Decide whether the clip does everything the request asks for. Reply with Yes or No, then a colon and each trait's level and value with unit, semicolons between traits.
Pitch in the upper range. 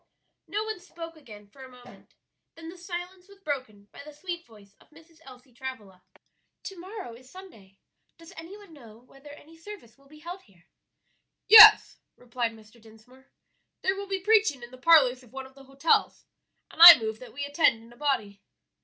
Yes: very high, 275 Hz